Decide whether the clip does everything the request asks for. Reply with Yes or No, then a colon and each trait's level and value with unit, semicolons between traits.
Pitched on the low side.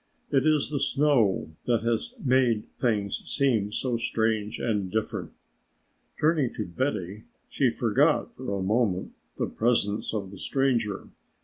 Yes: low, 115 Hz